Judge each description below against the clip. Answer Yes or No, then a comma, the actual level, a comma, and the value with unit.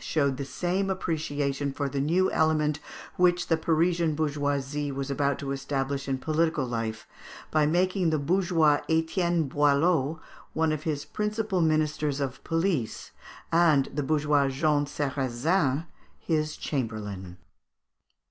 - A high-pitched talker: No, medium, 150 Hz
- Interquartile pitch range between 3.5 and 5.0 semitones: No, average, 2.9 semitones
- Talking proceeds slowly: Yes, slow, 130 wpm